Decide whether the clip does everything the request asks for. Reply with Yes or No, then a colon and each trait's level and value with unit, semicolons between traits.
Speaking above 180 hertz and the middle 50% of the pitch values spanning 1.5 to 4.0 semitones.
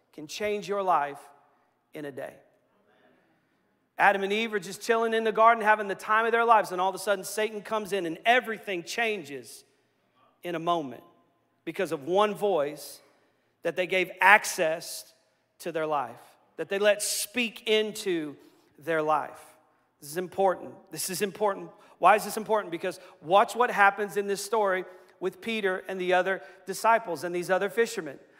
Yes: high, 190 Hz; average, 3.3 semitones